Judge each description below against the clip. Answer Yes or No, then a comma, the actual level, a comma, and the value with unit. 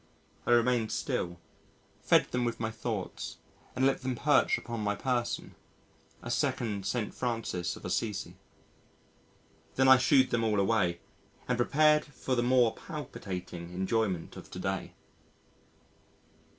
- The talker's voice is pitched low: Yes, low, 115 Hz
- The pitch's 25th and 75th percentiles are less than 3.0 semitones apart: No, average, 4.0 semitones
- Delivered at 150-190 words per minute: No, slow, 135 wpm